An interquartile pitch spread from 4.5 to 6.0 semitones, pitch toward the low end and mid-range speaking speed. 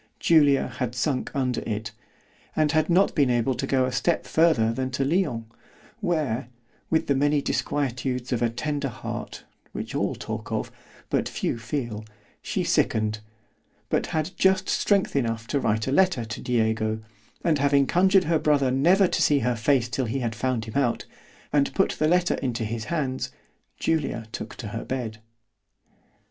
Yes: average, 4.8 semitones; low, 130 Hz; average, 160 wpm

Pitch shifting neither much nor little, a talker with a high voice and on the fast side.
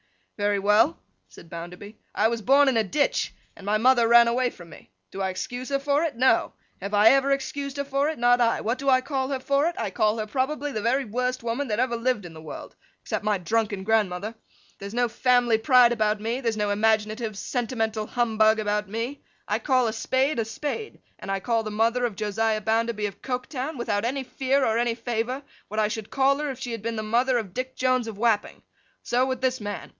Yes: average, 3.3 semitones; high, 230 Hz; fast, 225 wpm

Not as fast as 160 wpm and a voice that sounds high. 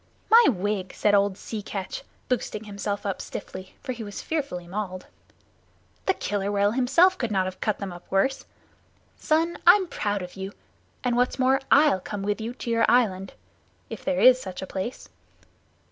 No: average, 175 wpm; high, 210 Hz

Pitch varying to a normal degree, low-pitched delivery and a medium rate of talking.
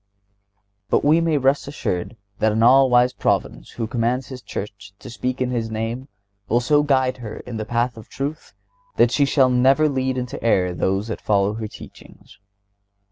Yes: average, 3.2 semitones; low, 125 Hz; average, 185 wpm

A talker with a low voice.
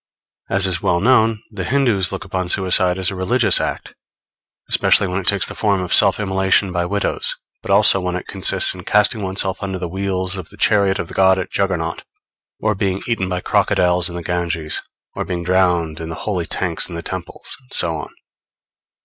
Yes: very low, 95 Hz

